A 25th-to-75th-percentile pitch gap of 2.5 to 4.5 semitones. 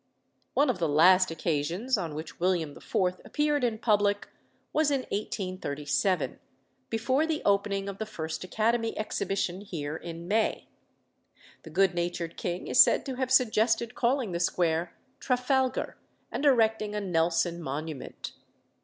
No: wide, 5.5 semitones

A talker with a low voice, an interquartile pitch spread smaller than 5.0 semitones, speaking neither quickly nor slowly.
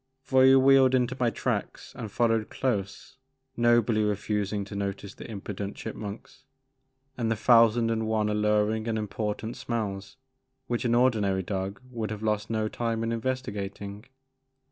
Yes: low, 110 Hz; narrow, 2.5 semitones; average, 145 wpm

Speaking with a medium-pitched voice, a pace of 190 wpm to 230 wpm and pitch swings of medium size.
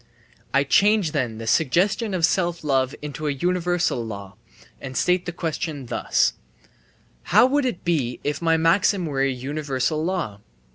No: medium, 155 Hz; average, 155 wpm; average, 4.9 semitones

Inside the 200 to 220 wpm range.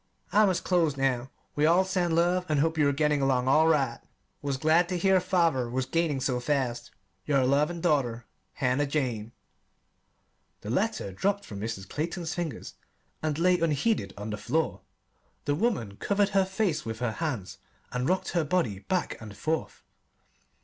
No: average, 170 wpm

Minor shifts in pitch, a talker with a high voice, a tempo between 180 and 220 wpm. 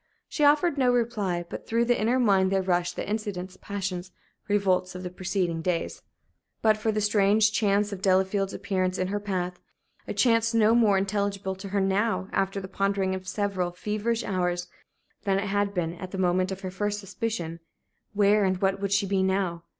Yes: narrow, 2.1 semitones; high, 195 Hz; average, 190 wpm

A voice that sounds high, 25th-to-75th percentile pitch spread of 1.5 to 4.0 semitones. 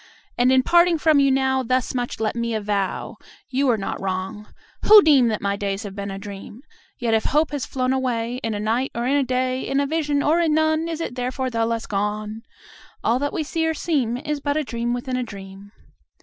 No: very high, 250 Hz; average, 4.7 semitones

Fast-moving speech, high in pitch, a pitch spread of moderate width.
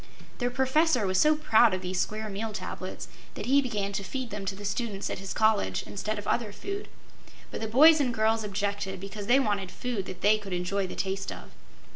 Yes: fast, 215 wpm; high, 210 Hz; average, 3.7 semitones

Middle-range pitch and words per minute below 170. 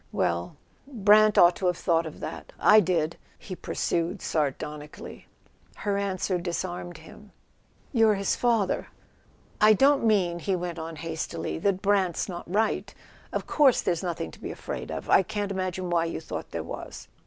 Yes: medium, 180 Hz; average, 160 wpm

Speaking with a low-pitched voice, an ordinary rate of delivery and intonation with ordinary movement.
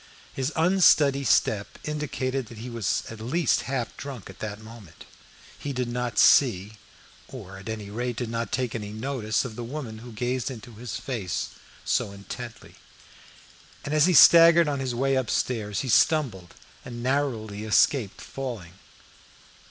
Yes: low, 120 Hz; average, 150 wpm; average, 3.8 semitones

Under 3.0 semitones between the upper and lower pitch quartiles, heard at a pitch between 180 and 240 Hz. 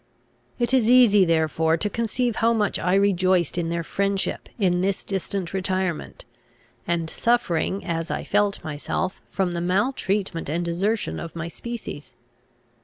No: average, 3.4 semitones; high, 190 Hz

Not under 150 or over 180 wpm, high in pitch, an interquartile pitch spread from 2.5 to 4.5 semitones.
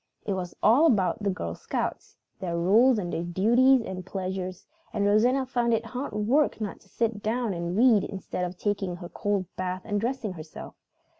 No: average, 190 wpm; high, 205 Hz; average, 4.1 semitones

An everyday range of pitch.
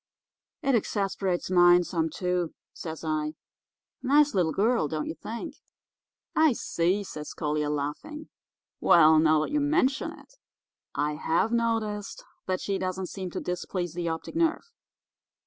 No: wide, 6.2 semitones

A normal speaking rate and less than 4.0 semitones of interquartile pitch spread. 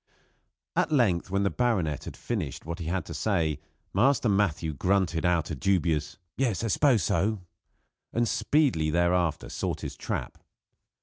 No: average, 150 wpm; average, 4.9 semitones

